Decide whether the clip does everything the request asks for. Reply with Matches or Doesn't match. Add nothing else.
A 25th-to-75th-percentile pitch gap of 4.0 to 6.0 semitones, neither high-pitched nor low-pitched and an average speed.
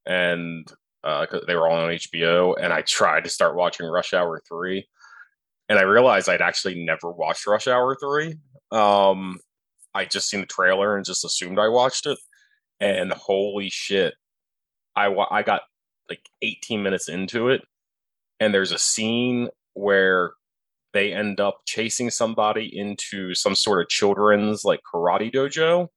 Doesn't match